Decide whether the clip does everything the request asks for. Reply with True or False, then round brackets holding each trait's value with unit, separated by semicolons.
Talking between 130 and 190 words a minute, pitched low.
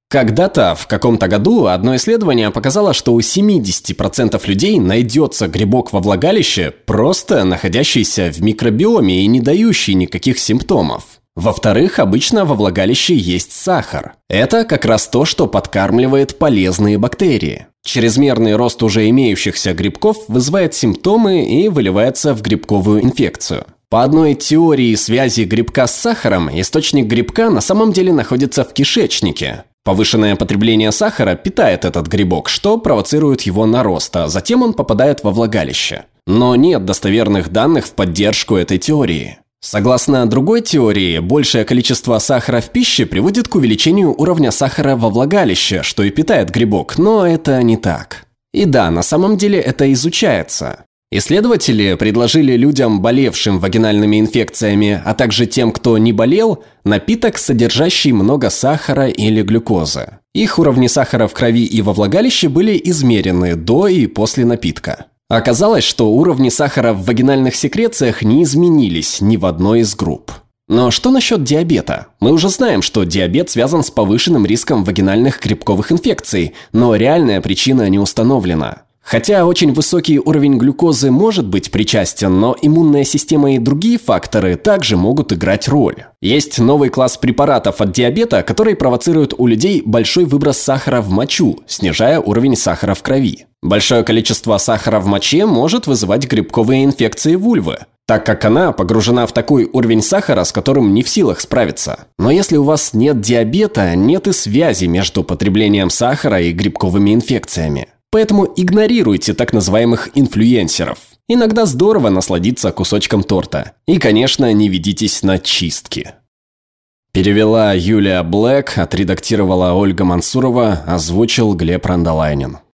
True (140 wpm; 115 Hz)